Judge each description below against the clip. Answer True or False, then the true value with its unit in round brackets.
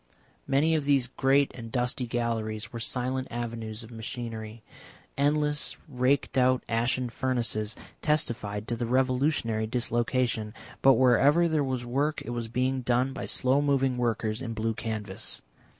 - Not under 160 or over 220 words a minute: False (145 wpm)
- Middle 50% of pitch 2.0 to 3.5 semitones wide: True (2.7 semitones)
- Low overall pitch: True (125 Hz)